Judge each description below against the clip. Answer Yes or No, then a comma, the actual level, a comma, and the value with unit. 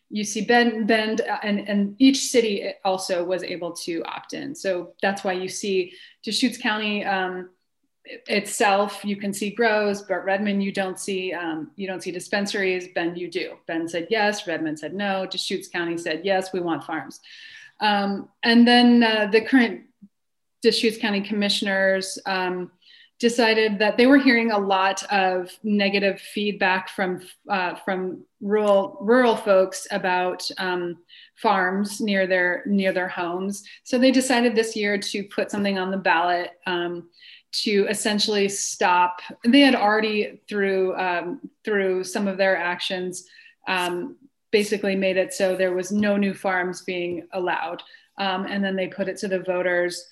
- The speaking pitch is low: No, high, 200 Hz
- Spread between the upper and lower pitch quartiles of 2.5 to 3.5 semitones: Yes, average, 2.8 semitones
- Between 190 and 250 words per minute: No, average, 160 wpm